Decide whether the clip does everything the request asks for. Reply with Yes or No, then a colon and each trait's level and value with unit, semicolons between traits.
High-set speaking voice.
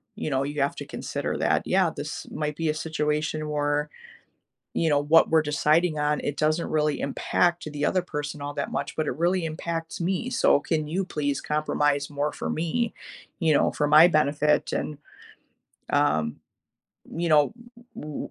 No: medium, 150 Hz